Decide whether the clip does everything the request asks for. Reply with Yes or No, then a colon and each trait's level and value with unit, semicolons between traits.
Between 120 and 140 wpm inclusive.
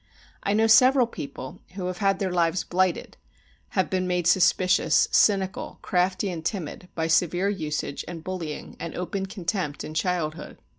No: average, 155 wpm